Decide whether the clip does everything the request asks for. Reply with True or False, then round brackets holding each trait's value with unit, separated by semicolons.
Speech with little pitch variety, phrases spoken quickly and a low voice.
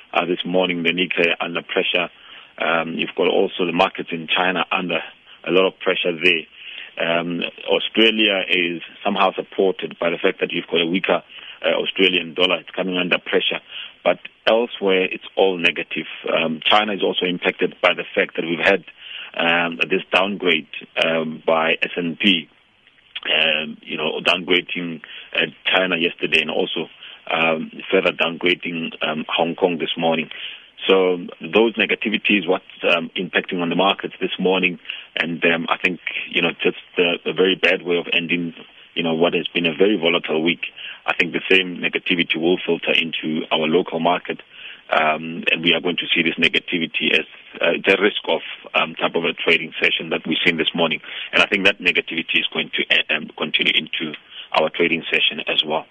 False (1.9 semitones; 180 wpm; 85 Hz)